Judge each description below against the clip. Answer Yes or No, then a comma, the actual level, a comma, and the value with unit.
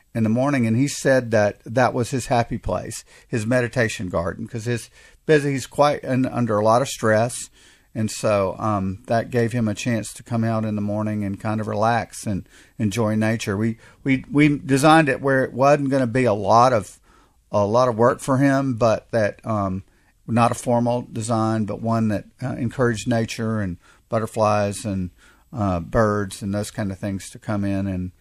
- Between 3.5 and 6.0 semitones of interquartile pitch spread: No, average, 3.0 semitones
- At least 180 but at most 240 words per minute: Yes, average, 200 wpm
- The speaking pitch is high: No, low, 115 Hz